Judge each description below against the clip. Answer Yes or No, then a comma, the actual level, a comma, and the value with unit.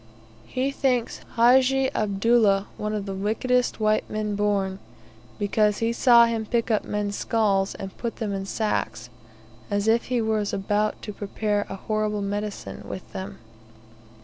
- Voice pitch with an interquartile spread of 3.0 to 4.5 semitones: No, narrow, 2.4 semitones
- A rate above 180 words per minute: No, average, 150 wpm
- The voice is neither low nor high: No, high, 210 Hz